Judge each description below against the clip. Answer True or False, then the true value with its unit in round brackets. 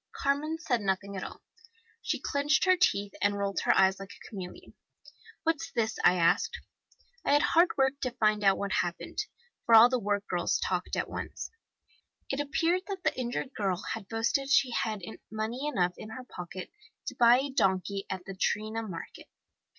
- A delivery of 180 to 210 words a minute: True (185 wpm)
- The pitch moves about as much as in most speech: False (6.0 semitones)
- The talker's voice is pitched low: False (220 Hz)